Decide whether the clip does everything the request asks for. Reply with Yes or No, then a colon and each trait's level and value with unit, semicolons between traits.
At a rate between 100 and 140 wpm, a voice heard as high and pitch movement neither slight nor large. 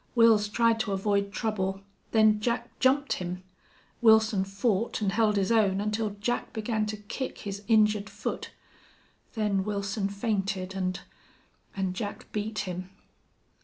No: slow, 135 wpm; high, 210 Hz; narrow, 2.0 semitones